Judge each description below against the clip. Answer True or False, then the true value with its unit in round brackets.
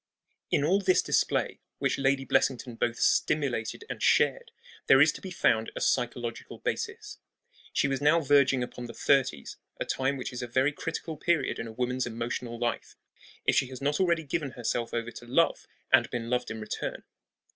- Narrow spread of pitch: False (3.2 semitones)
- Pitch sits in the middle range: False (130 Hz)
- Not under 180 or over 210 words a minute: True (185 wpm)